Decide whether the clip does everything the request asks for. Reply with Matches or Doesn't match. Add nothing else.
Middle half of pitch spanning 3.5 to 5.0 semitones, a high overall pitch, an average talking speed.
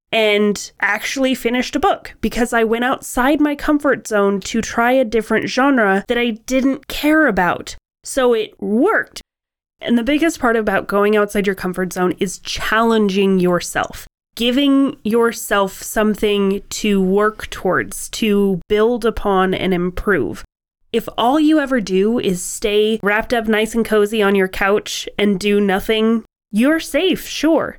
Matches